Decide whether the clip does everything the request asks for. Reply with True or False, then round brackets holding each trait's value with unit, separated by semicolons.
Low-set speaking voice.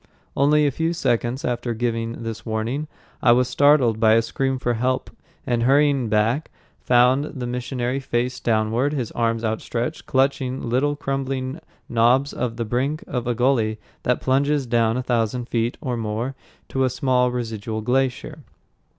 True (125 Hz)